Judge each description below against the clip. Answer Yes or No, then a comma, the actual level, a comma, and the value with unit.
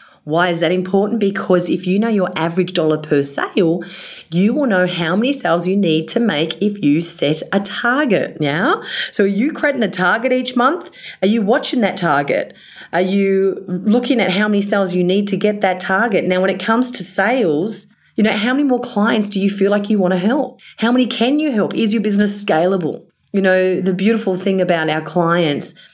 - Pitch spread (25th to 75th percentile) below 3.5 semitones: No, average, 3.8 semitones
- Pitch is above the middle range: Yes, high, 195 Hz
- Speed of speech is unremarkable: No, fast, 215 wpm